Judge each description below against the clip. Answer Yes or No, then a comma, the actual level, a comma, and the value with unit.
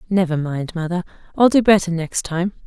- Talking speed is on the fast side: No, average, 180 wpm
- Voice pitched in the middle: Yes, medium, 175 Hz